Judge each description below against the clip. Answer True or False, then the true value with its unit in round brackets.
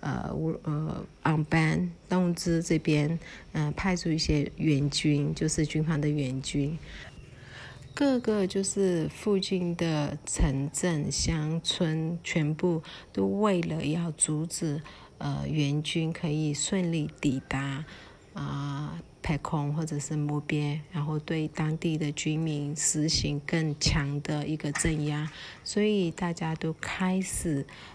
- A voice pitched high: False (155 Hz)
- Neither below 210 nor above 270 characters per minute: False (185 characters per minute)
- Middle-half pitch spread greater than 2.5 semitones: False (2.2 semitones)